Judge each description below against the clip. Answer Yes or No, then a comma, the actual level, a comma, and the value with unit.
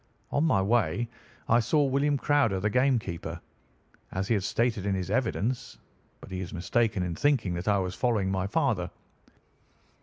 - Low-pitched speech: Yes, low, 110 Hz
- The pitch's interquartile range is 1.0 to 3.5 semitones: No, average, 5.0 semitones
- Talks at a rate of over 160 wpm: Yes, average, 175 wpm